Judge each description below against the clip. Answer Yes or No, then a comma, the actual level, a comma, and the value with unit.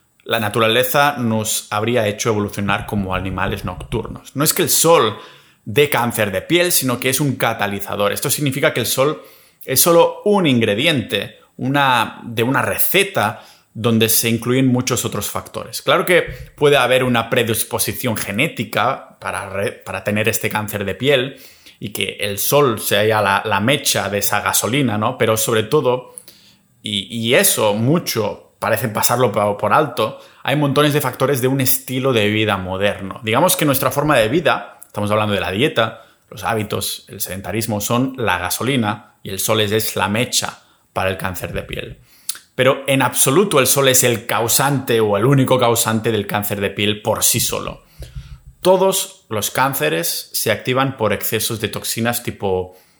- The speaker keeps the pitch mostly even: No, average, 4.2 semitones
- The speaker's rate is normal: Yes, average, 170 wpm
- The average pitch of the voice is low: Yes, low, 115 Hz